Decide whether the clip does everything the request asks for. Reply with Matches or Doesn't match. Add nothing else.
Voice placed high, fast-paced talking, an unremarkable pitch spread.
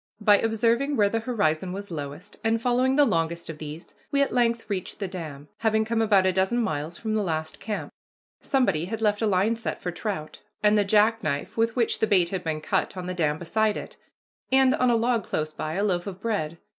Matches